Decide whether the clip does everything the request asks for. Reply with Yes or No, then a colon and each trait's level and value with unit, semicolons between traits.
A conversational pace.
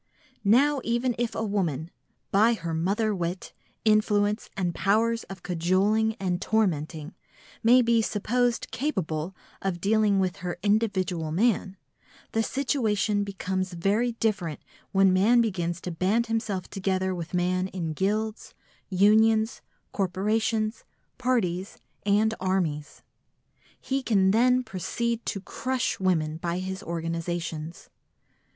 No: slow, 120 wpm